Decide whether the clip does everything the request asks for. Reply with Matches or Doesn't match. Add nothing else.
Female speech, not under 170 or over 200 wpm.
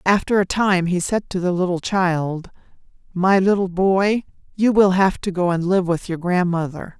Matches